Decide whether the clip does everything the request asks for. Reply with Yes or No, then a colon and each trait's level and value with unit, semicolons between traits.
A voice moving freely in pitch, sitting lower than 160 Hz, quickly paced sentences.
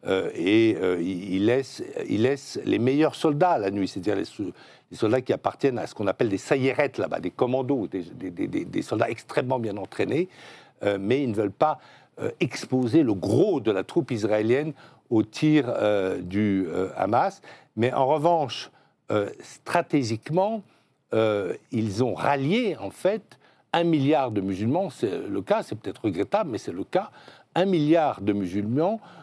No: wide, 7.1 semitones; medium, 140 Hz; average, 175 wpm